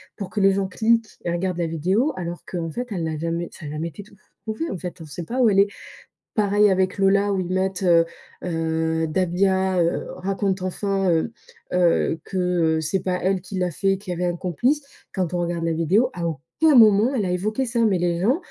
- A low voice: No, medium, 185 Hz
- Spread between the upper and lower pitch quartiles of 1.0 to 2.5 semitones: No, average, 2.9 semitones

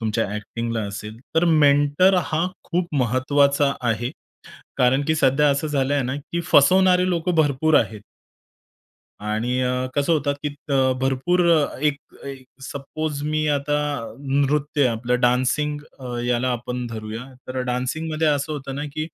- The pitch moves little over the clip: No, average, 3.3 semitones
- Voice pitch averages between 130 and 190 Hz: Yes, medium, 140 Hz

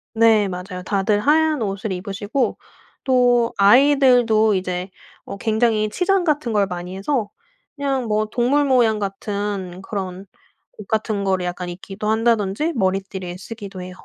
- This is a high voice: Yes, high, 210 Hz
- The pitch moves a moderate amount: Yes, average, 3.9 semitones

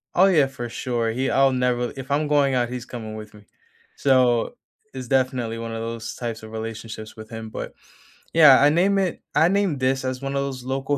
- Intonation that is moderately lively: Yes, average, 3.3 semitones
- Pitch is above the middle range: No, low, 130 Hz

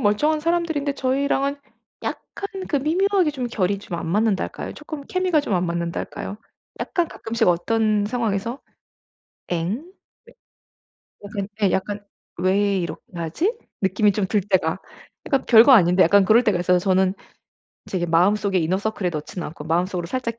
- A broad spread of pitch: Yes, wide, 6.6 semitones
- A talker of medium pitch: No, high, 205 Hz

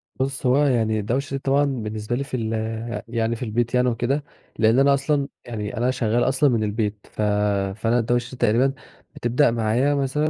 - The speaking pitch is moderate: No, low, 120 Hz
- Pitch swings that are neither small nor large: Yes, average, 3.4 semitones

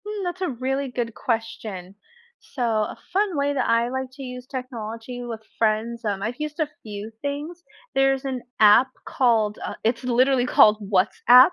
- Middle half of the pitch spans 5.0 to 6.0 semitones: No, average, 3.4 semitones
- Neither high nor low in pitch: No, high, 245 Hz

